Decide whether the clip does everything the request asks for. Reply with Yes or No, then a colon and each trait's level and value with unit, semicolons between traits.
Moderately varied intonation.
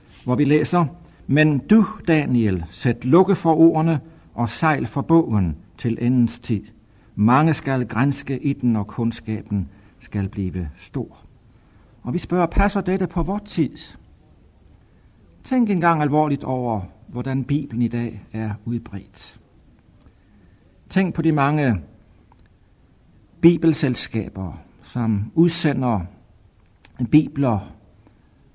No: wide, 6.9 semitones